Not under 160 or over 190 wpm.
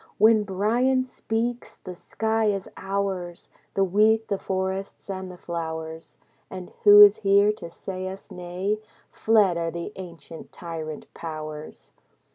No: slow, 135 wpm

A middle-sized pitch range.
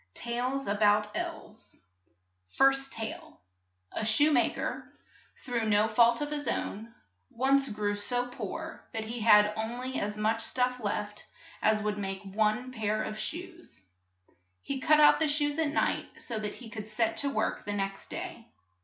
Yes: average, 4.2 semitones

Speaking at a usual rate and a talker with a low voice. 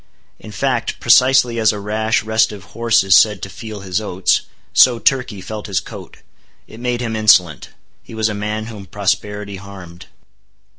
Yes: average, 165 wpm; low, 105 Hz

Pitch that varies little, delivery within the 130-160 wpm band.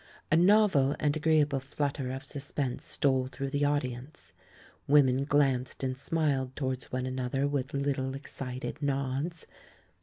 Yes: narrow, 1.8 semitones; average, 145 wpm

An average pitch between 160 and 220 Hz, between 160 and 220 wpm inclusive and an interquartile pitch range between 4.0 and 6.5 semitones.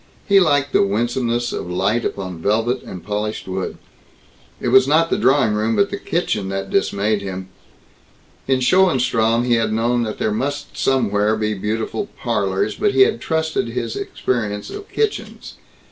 No: low, 115 Hz; average, 165 wpm; average, 4.7 semitones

